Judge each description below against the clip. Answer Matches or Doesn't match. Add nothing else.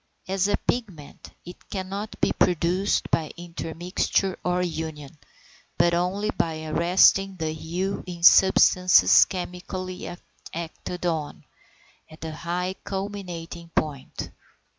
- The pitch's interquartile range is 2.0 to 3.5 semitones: Matches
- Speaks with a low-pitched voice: Doesn't match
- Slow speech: Matches